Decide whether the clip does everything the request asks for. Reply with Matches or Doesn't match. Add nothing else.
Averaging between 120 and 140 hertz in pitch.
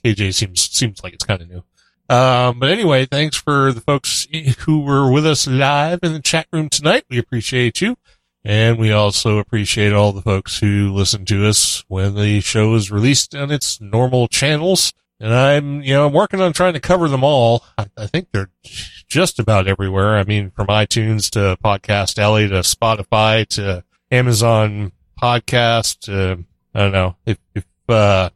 Doesn't match